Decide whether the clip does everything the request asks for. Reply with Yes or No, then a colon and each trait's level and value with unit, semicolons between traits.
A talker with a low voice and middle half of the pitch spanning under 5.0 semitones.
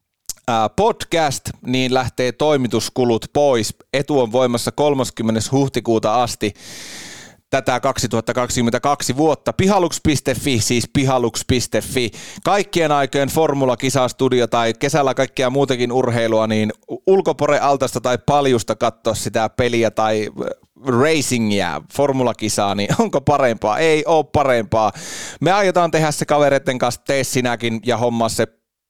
Yes: low, 125 Hz; average, 3.8 semitones